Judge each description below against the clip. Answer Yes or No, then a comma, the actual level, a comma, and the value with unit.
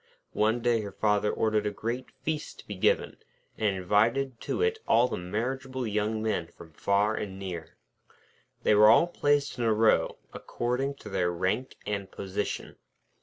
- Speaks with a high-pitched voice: No, low, 110 Hz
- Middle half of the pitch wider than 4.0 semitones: No, average, 3.7 semitones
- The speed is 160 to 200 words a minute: Yes, average, 170 wpm